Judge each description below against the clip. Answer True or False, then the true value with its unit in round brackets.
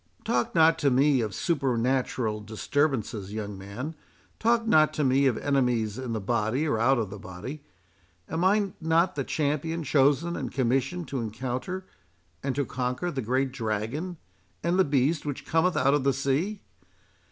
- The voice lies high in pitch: False (135 Hz)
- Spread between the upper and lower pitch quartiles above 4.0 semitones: True (5.1 semitones)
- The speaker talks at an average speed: True (165 wpm)